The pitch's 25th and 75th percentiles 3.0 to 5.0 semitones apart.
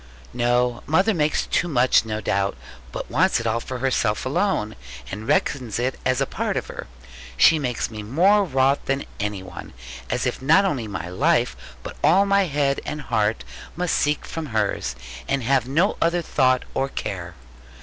No: wide, 5.5 semitones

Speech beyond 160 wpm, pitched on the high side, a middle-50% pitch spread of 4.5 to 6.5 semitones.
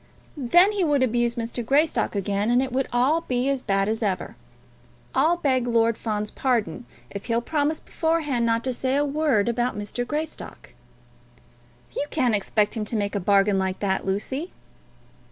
Yes: average, 170 wpm; high, 240 Hz; average, 5.1 semitones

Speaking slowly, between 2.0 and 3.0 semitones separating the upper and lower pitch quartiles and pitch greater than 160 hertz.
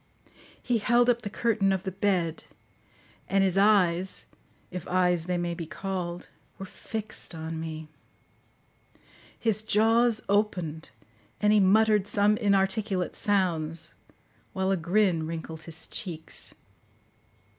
No: slow, 125 wpm; average, 3.6 semitones; high, 190 Hz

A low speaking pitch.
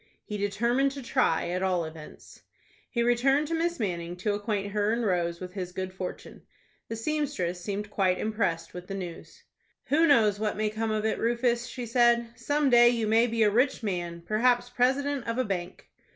No: high, 215 Hz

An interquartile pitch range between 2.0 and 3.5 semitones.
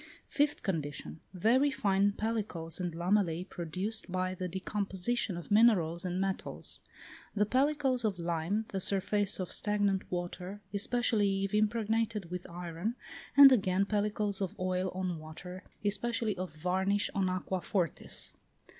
Yes: average, 2.8 semitones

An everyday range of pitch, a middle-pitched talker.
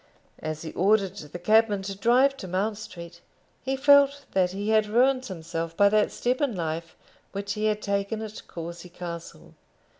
No: average, 4.4 semitones; high, 200 Hz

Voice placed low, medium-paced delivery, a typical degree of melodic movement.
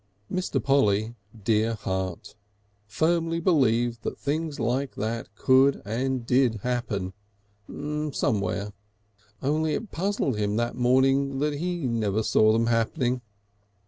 No: low, 125 Hz; slow, 115 wpm; average, 4.6 semitones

